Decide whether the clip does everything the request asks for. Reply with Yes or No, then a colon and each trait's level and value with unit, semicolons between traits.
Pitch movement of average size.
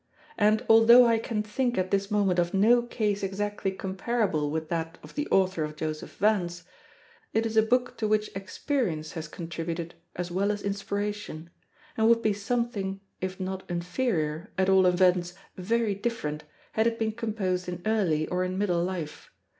Yes: average, 3.9 semitones